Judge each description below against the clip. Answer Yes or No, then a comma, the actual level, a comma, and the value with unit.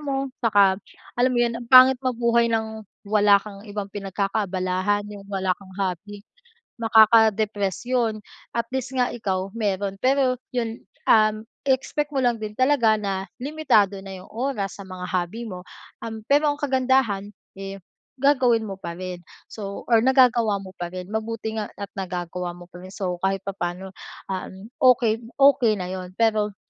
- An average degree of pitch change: Yes, average, 3.7 semitones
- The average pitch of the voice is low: No, high, 210 Hz